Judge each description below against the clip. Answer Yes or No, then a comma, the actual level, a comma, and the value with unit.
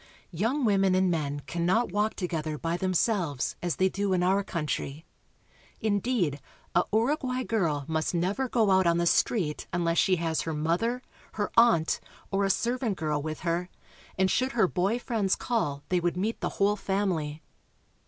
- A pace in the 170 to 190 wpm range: Yes, average, 175 wpm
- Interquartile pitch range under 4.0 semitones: No, average, 4.6 semitones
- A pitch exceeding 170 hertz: Yes, medium, 185 Hz